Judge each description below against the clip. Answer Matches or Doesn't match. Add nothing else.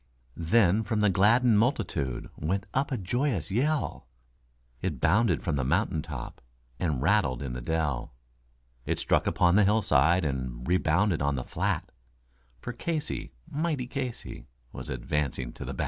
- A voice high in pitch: Doesn't match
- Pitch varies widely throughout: Matches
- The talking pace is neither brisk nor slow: Matches